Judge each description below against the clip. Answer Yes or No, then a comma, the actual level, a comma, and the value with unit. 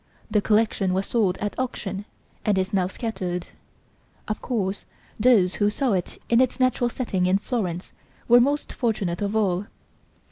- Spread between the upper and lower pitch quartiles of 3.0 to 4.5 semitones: Yes, average, 3.9 semitones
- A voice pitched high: Yes, high, 210 Hz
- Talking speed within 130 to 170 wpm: Yes, average, 155 wpm